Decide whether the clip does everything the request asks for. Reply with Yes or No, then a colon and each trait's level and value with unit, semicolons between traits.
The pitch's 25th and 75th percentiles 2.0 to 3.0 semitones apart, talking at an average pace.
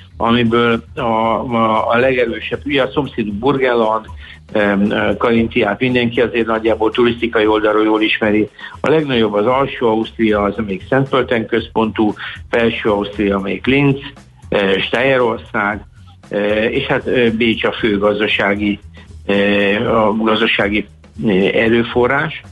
Yes: narrow, 2.4 semitones; average, 125 wpm